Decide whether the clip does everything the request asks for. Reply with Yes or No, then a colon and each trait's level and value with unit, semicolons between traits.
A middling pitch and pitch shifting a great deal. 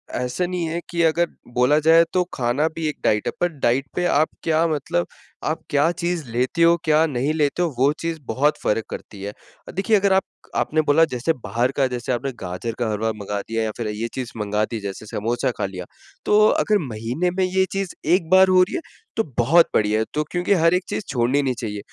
Yes: medium, 145 Hz; wide, 6.7 semitones